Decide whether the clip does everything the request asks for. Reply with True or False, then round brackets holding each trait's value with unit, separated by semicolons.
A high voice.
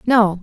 True (210 Hz)